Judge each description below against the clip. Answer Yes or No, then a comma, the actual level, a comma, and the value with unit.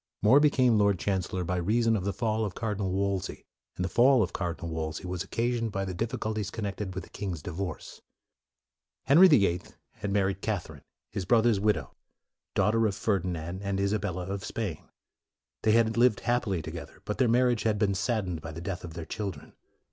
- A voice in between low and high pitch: No, low, 100 Hz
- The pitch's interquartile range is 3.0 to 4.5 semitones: Yes, average, 3.5 semitones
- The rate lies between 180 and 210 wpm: Yes, average, 195 wpm